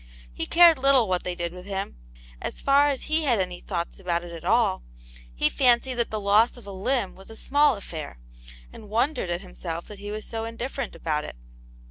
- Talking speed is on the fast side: Yes, fast, 210 wpm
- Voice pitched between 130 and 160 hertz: No, high, 210 Hz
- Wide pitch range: Yes, wide, 5.8 semitones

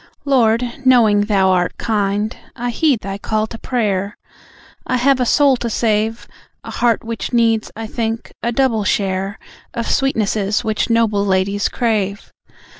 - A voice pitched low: No, high, 220 Hz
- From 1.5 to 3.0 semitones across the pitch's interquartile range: Yes, average, 2.7 semitones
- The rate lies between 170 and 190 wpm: No, average, 150 wpm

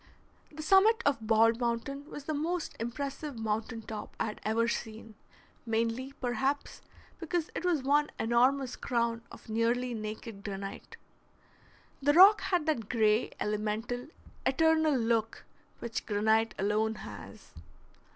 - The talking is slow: Yes, slow, 130 wpm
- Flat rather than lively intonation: No, average, 4.6 semitones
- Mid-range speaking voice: No, high, 235 Hz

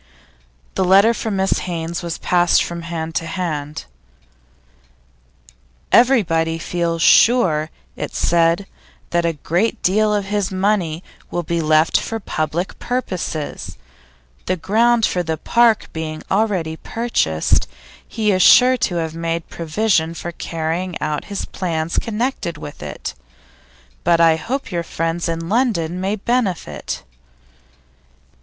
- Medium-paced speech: No, slow, 130 wpm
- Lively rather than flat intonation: No, average, 4.2 semitones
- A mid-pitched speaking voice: Yes, medium, 175 Hz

